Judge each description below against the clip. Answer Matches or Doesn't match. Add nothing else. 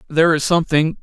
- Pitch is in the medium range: Matches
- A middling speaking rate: Matches